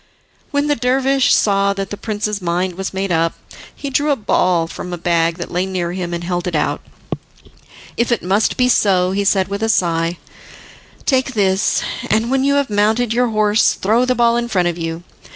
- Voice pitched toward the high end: Yes, high, 200 Hz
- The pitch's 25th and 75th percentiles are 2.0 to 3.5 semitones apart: No, average, 5.0 semitones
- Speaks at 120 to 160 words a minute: No, fast, 205 wpm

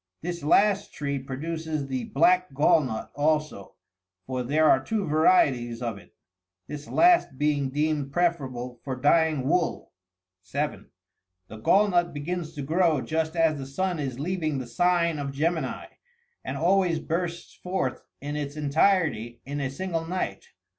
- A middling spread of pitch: Yes, average, 4.3 semitones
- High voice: No, medium, 150 Hz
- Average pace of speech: Yes, average, 155 wpm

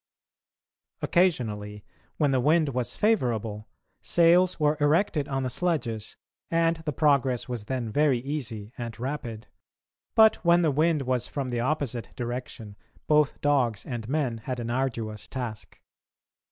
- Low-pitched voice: Yes, low, 130 Hz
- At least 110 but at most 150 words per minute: Yes, average, 140 wpm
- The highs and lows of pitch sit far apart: No, average, 4.5 semitones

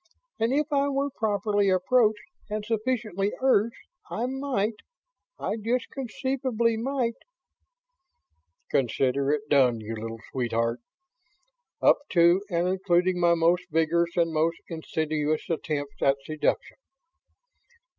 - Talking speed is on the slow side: Yes, slow, 115 wpm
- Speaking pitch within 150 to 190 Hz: Yes, medium, 185 Hz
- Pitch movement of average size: No, wide, 7.1 semitones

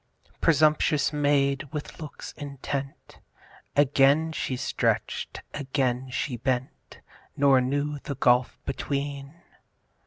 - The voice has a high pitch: No, medium, 140 Hz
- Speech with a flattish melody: Yes, narrow, 1.7 semitones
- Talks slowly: Yes, slow, 95 wpm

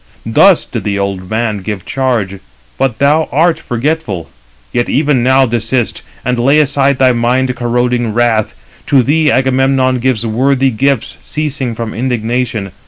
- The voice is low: Yes, low, 125 Hz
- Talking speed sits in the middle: Yes, average, 145 wpm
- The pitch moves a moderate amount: Yes, average, 3.1 semitones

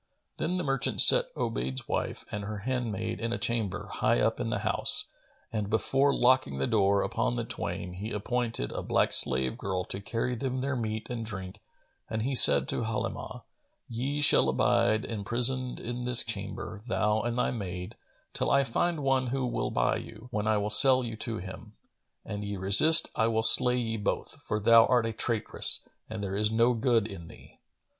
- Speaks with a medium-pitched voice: No, low, 110 Hz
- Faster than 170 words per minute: Yes, average, 190 wpm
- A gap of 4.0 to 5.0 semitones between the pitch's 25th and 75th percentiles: No, average, 3.4 semitones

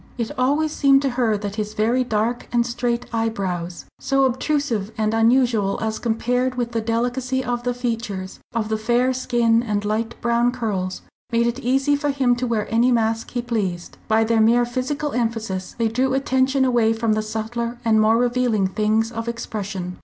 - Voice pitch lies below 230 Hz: No, high, 235 Hz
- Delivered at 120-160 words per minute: No, average, 185 wpm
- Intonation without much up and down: Yes, narrow, 2.3 semitones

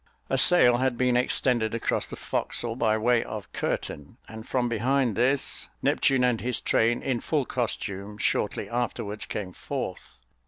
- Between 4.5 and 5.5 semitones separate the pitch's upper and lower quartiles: No, narrow, 2.5 semitones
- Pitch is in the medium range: No, low, 120 Hz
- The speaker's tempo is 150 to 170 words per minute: Yes, average, 155 wpm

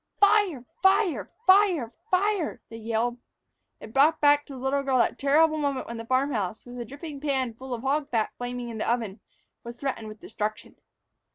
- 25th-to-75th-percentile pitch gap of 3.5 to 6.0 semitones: Yes, average, 4.2 semitones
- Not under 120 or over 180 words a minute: No, average, 190 wpm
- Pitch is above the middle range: Yes, very high, 260 Hz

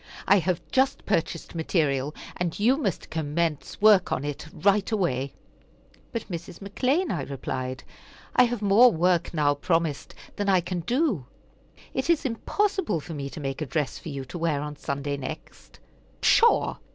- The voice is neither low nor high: Yes, medium, 170 Hz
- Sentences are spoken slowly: No, average, 165 wpm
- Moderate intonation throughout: No, wide, 6.0 semitones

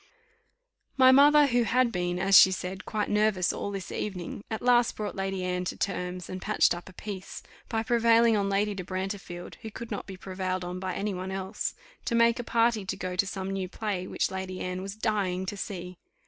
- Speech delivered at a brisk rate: Yes, fast, 215 wpm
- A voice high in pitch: Yes, high, 195 Hz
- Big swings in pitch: No, average, 2.9 semitones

